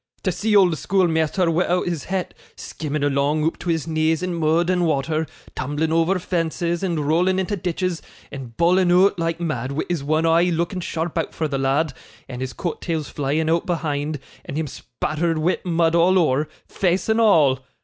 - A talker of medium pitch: Yes, medium, 165 Hz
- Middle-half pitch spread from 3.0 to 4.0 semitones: No, narrow, 2.5 semitones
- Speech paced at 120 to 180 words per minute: No, average, 190 wpm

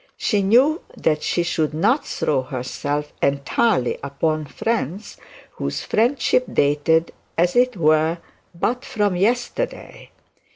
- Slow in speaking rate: Yes, slow, 115 wpm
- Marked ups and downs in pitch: Yes, wide, 7.5 semitones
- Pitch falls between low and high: Yes, medium, 165 Hz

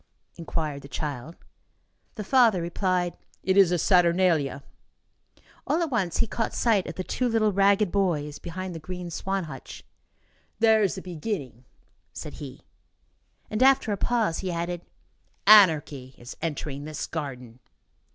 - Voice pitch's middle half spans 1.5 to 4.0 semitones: No, average, 4.9 semitones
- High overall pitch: No, medium, 180 Hz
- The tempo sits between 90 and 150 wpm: Yes, average, 145 wpm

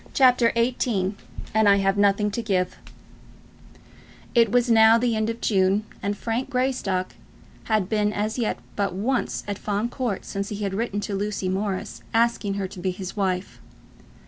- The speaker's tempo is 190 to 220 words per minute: No, average, 170 wpm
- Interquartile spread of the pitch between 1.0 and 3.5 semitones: Yes, average, 3.0 semitones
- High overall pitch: Yes, high, 210 Hz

